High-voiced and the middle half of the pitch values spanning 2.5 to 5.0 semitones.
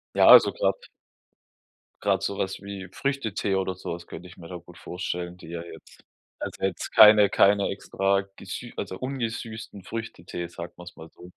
No: very low, 95 Hz; average, 2.8 semitones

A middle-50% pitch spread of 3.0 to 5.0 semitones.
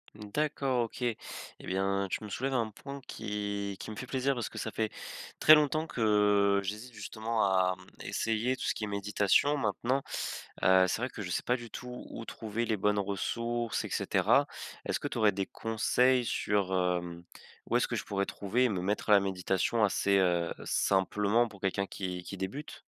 Yes: average, 3.4 semitones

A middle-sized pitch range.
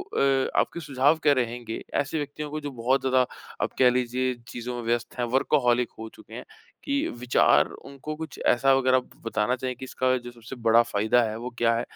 No: narrow, 2.3 semitones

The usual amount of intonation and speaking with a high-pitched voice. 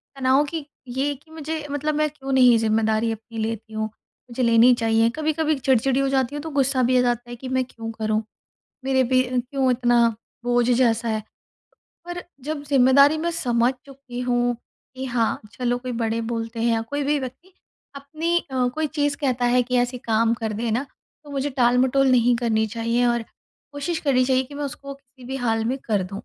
Yes: average, 3.1 semitones; very high, 250 Hz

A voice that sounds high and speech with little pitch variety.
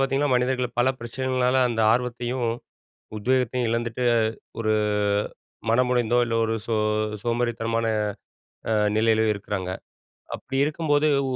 No: low, 120 Hz; narrow, 2.0 semitones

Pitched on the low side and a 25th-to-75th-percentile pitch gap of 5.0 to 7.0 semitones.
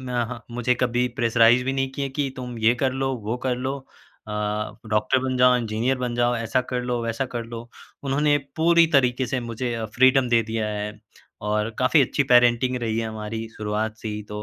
No: low, 120 Hz; narrow, 2.4 semitones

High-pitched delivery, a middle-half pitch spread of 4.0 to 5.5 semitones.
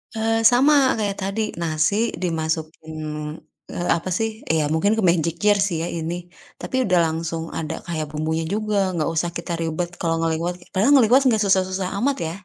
No: medium, 175 Hz; average, 4.5 semitones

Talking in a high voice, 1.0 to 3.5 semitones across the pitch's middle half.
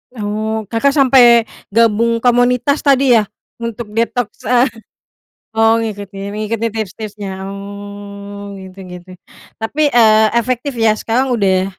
Yes: high, 220 Hz; average, 2.9 semitones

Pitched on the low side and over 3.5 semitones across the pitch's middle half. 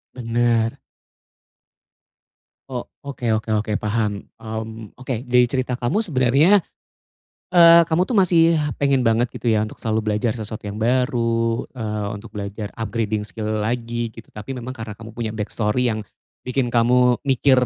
No: low, 115 Hz; average, 2.8 semitones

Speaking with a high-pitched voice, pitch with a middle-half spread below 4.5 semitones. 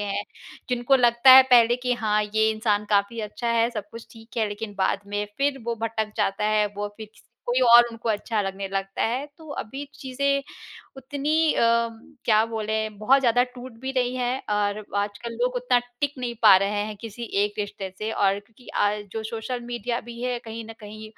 Yes: high, 225 Hz; average, 2.9 semitones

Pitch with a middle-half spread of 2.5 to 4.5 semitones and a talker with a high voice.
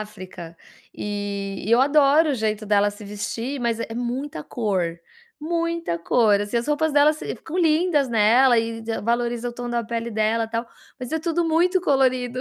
No: average, 5.3 semitones; high, 235 Hz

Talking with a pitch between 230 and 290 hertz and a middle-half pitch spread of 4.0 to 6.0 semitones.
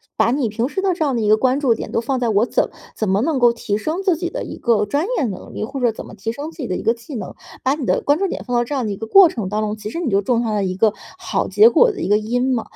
Yes: high, 240 Hz; average, 5.1 semitones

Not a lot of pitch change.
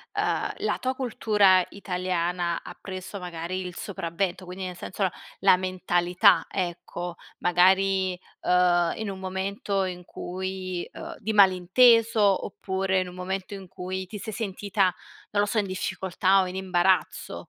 Yes: narrow, 1.5 semitones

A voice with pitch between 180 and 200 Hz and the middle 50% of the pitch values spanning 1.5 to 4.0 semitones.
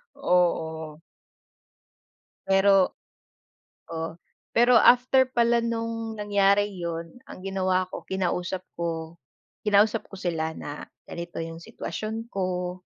No: high, 190 Hz; average, 4.6 semitones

